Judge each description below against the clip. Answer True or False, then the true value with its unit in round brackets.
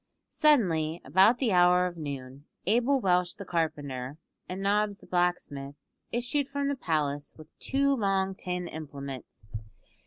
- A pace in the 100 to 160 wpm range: True (135 wpm)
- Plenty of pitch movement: True (6.1 semitones)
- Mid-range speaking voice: True (180 Hz)